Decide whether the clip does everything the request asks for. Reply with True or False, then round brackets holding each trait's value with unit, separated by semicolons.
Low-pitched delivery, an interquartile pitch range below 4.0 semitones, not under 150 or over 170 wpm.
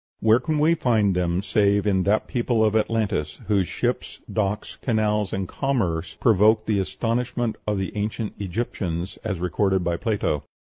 True (105 Hz; 2.9 semitones; 155 wpm)